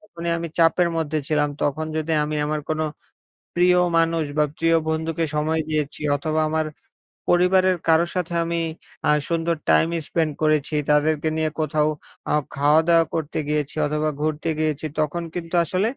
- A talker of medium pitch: Yes, medium, 160 Hz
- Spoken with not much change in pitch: Yes, narrow, 1.5 semitones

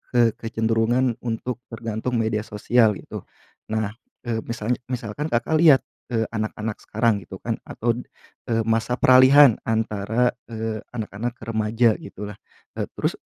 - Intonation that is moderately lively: No, narrow, 1.8 semitones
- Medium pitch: No, low, 115 Hz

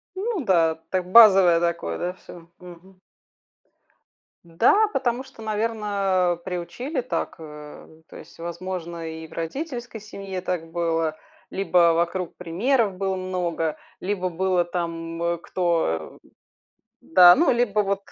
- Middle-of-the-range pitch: Yes, medium, 180 Hz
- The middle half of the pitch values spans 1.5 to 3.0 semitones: No, average, 3.5 semitones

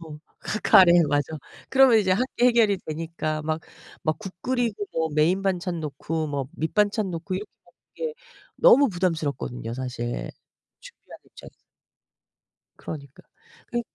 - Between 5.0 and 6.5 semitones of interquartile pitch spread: Yes, wide, 5.5 semitones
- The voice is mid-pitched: Yes, medium, 175 Hz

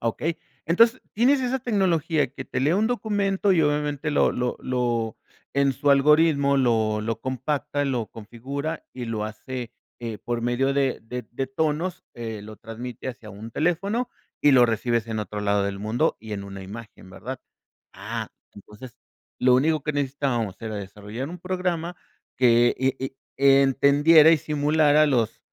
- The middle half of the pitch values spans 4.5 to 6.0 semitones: Yes, average, 5.0 semitones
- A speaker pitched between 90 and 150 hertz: Yes, low, 135 Hz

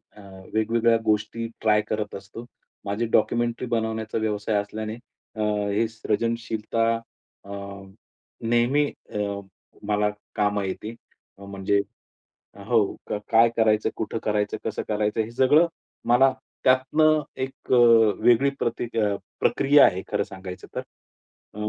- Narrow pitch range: Yes, narrow, 2.1 semitones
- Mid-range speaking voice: No, low, 110 Hz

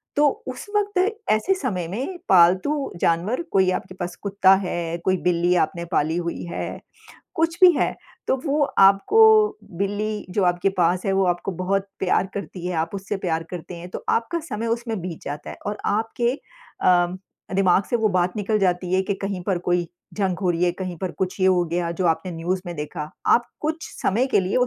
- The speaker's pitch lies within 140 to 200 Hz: Yes, high, 190 Hz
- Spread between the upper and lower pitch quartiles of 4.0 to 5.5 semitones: Yes, average, 4.3 semitones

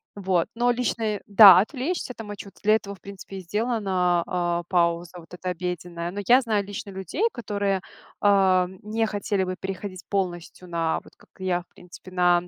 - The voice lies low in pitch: No, high, 190 Hz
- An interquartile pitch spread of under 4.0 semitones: Yes, narrow, 2.6 semitones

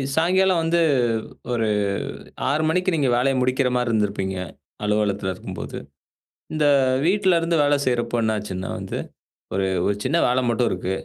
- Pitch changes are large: Yes, wide, 7.7 semitones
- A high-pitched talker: No, low, 125 Hz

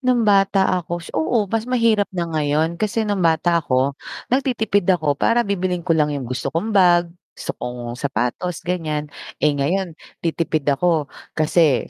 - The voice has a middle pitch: Yes, medium, 170 Hz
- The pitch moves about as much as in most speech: Yes, average, 4.9 semitones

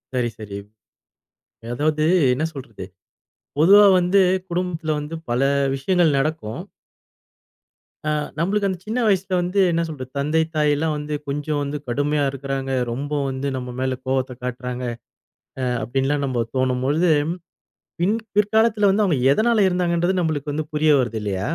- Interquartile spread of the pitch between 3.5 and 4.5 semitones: No, average, 5.3 semitones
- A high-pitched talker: No, medium, 150 Hz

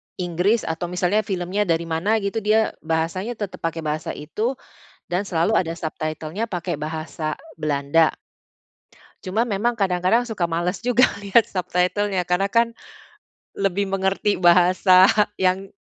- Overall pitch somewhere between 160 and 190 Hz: Yes, medium, 185 Hz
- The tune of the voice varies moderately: Yes, average, 3.7 semitones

